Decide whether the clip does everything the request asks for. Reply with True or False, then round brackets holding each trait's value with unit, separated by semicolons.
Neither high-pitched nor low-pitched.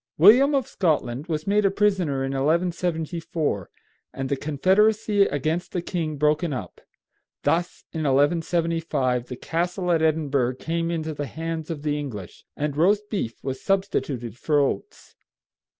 True (160 Hz)